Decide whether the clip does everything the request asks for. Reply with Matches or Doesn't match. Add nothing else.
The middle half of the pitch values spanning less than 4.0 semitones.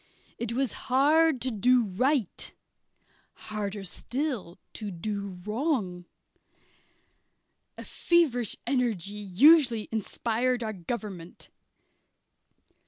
Doesn't match